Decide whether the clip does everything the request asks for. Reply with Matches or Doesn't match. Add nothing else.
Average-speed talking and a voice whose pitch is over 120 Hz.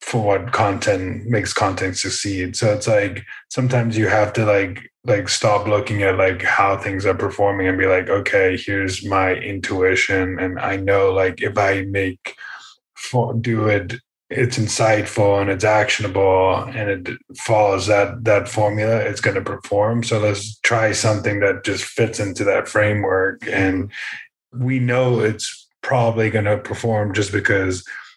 Doesn't match